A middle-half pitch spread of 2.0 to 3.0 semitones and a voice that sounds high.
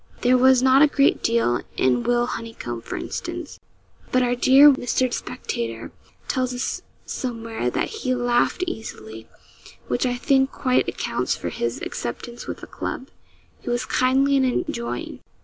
Yes: narrow, 2.4 semitones; high, 245 Hz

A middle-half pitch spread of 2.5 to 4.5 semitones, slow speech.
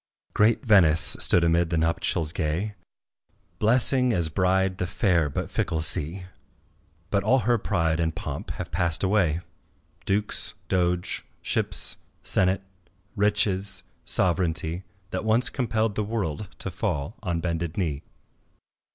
Yes: average, 4.1 semitones; slow, 125 wpm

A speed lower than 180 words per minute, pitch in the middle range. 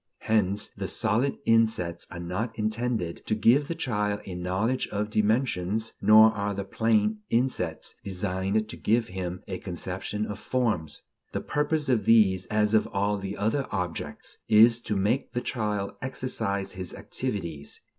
No: average, 155 wpm; low, 105 Hz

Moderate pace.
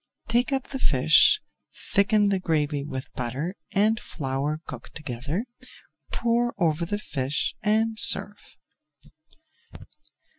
No: slow, 110 wpm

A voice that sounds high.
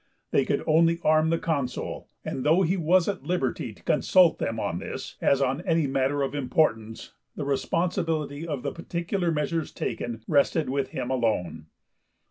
No: medium, 150 Hz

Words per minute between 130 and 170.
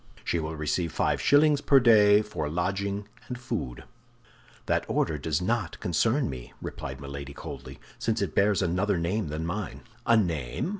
Yes: average, 160 wpm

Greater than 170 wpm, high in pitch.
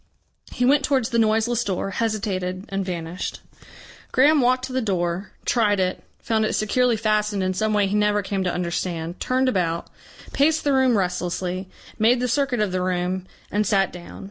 Yes: average, 180 wpm; high, 210 Hz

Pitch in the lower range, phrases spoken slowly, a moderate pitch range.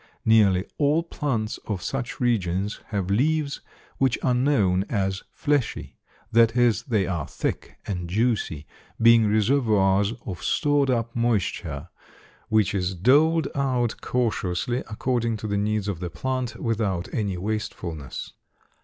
Yes: low, 110 Hz; slow, 130 wpm; average, 4.5 semitones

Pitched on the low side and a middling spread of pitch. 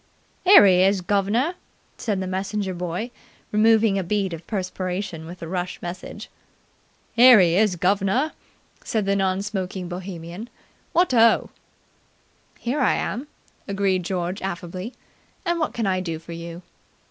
No: high, 190 Hz; average, 3.2 semitones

